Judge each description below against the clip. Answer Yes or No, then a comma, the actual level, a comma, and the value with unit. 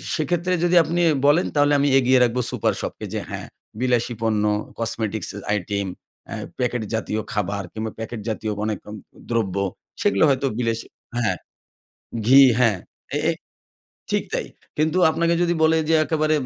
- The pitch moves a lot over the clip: Yes, wide, 5.9 semitones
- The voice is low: Yes, low, 120 Hz